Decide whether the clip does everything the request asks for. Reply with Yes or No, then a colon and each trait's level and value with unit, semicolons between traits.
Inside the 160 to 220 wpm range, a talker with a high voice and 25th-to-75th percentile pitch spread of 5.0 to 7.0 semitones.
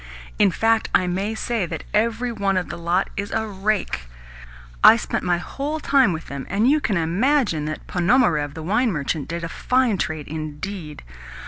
Yes: average, 185 wpm; high, 195 Hz; wide, 5.5 semitones